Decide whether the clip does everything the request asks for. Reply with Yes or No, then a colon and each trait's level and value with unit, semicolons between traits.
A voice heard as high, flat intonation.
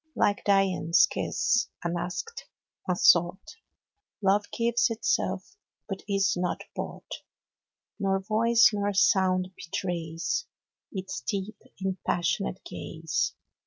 Yes: high, 195 Hz; narrow, 2.3 semitones